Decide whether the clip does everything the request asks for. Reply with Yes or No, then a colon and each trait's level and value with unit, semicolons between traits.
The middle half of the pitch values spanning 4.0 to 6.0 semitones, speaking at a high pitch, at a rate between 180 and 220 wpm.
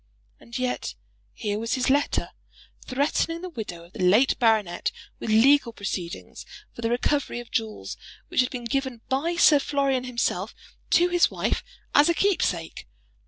No: average, 4.5 semitones; very high, 250 Hz; average, 160 wpm